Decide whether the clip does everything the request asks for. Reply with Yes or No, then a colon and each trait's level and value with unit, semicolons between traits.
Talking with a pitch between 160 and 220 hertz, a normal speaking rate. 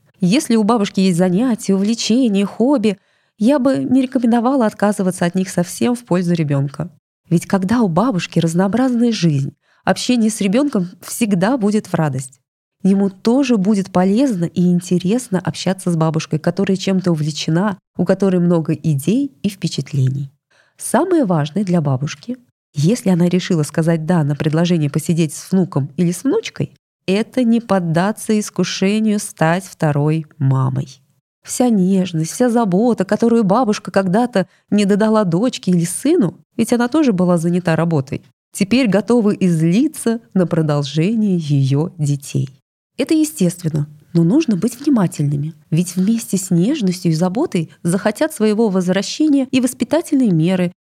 Yes: high, 190 Hz; average, 135 wpm